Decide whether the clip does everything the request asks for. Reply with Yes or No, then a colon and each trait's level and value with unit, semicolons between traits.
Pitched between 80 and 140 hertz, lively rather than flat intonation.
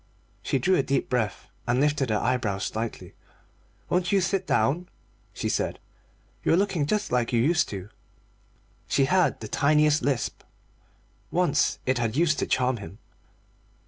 Yes: low, 135 Hz; wide, 6.3 semitones